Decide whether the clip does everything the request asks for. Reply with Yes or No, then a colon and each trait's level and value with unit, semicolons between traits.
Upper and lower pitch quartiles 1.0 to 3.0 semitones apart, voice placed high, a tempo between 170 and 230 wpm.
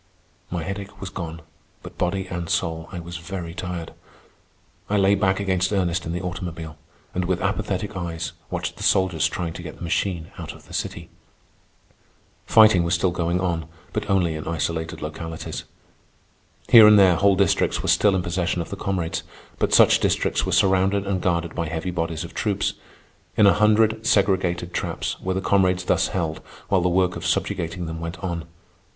No: narrow, 2.5 semitones; very low, 90 Hz; average, 180 wpm